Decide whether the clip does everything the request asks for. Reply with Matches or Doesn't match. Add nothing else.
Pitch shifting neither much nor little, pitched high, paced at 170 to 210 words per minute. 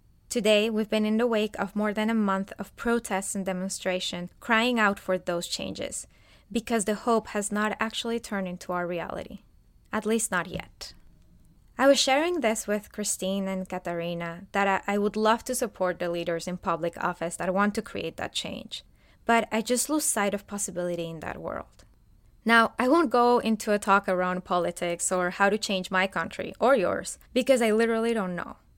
Matches